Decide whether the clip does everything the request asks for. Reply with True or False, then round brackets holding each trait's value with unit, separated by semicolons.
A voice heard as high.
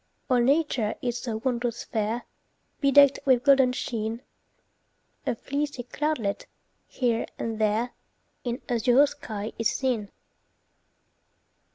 True (245 Hz)